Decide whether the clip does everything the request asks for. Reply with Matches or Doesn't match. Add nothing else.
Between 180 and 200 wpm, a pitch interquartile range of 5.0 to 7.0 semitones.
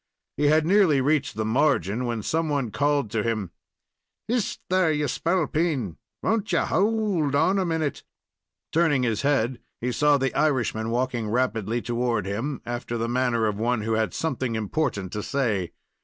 Doesn't match